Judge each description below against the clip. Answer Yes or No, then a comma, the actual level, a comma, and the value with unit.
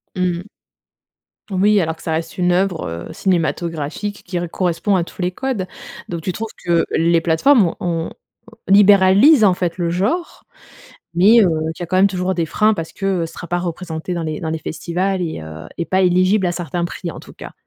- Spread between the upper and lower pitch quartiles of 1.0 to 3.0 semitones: Yes, narrow, 2.5 semitones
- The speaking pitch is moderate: Yes, medium, 180 Hz